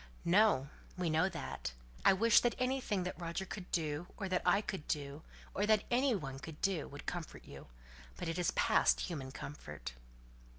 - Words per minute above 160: Yes, average, 180 wpm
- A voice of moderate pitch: Yes, medium, 175 Hz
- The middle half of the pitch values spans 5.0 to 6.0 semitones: Yes, wide, 5.4 semitones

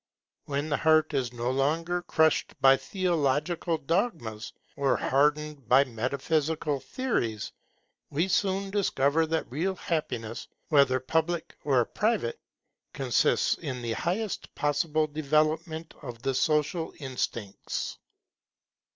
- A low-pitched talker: No, medium, 150 Hz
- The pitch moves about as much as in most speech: Yes, average, 3.9 semitones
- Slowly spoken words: Yes, slow, 110 wpm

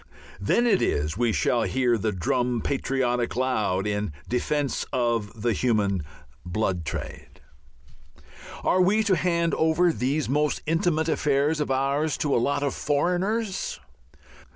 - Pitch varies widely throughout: Yes, wide, 6.1 semitones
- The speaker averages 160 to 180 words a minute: No, slow, 135 wpm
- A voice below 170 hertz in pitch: Yes, low, 135 Hz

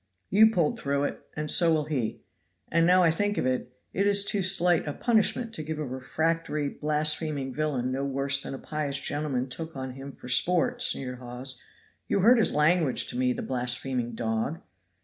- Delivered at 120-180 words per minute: No, average, 190 wpm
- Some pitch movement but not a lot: Yes, average, 4.3 semitones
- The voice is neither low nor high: Yes, medium, 150 Hz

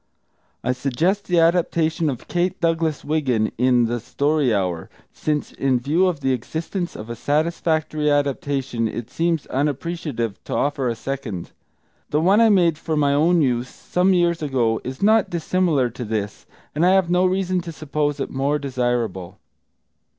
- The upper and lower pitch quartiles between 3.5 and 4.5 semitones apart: No, average, 5.1 semitones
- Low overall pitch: No, medium, 145 Hz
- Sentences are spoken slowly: No, average, 165 wpm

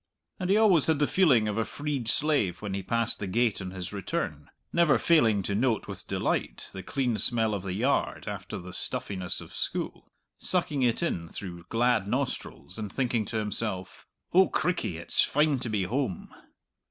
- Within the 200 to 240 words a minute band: No, average, 185 wpm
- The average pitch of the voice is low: Yes, low, 115 Hz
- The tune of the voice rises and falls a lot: Yes, wide, 6.4 semitones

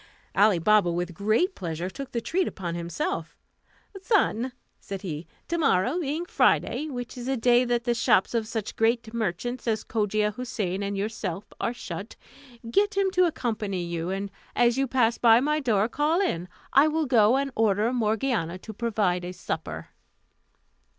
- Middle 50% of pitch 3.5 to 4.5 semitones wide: No, average, 4.9 semitones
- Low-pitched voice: No, high, 225 Hz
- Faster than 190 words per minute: No, average, 170 wpm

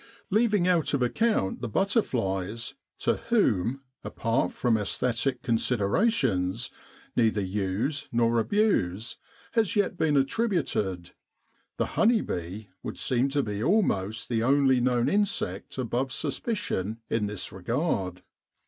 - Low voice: Yes, low, 120 Hz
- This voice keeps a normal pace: No, slow, 120 wpm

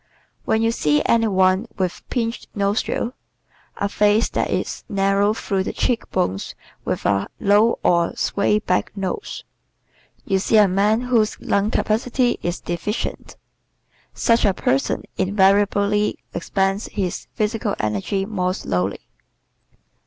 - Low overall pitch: No, high, 200 Hz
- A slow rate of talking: Yes, slow, 130 wpm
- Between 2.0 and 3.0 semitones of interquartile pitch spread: Yes, narrow, 2.6 semitones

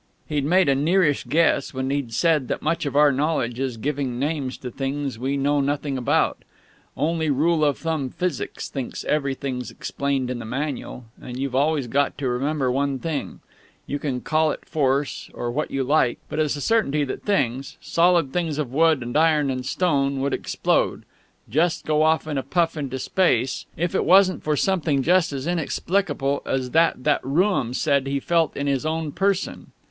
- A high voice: No, medium, 145 Hz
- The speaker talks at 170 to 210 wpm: Yes, average, 185 wpm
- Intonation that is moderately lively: Yes, average, 3.1 semitones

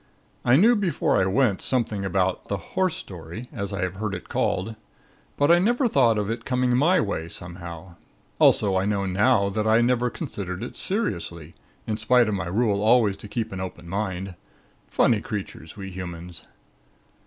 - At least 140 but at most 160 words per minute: No, average, 175 wpm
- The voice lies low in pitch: Yes, low, 105 Hz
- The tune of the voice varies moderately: Yes, average, 4.7 semitones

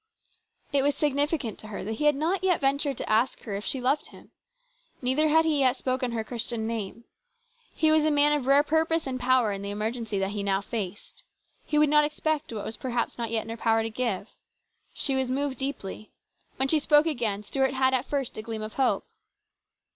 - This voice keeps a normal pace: No, fast, 215 wpm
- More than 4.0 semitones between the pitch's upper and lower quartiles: Yes, average, 4.7 semitones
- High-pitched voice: Yes, very high, 255 Hz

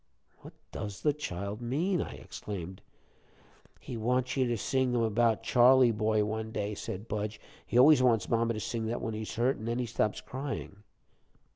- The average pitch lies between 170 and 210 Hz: No, low, 115 Hz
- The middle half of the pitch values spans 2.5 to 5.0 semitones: Yes, average, 2.9 semitones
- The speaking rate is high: No, average, 190 wpm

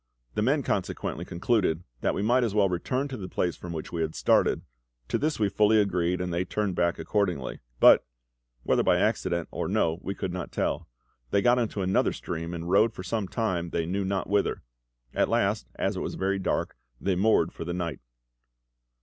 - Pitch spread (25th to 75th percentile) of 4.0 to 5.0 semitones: No, average, 3.5 semitones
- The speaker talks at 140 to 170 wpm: No, average, 200 wpm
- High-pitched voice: No, very low, 95 Hz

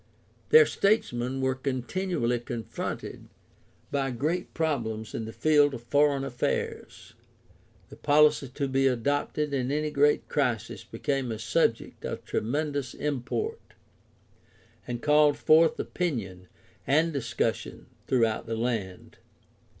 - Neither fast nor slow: No, slow, 115 wpm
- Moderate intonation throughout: Yes, average, 3.9 semitones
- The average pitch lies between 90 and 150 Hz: Yes, low, 135 Hz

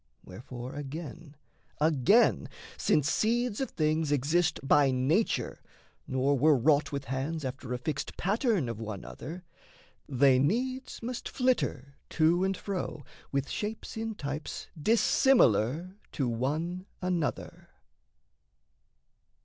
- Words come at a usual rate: No, slow, 115 wpm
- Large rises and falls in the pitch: Yes, wide, 6.1 semitones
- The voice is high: No, medium, 155 Hz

